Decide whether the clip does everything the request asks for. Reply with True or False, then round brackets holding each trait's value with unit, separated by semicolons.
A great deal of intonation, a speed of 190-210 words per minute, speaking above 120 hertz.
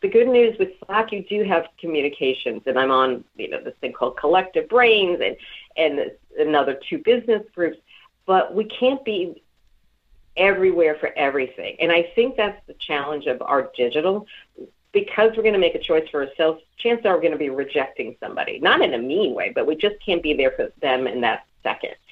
True (7.5 semitones; 200 wpm; 190 Hz)